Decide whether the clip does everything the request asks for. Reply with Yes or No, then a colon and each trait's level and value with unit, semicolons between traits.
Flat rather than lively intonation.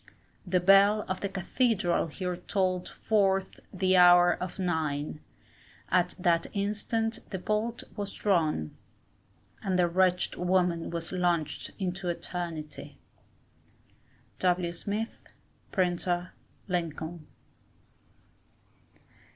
Yes: narrow, 2.1 semitones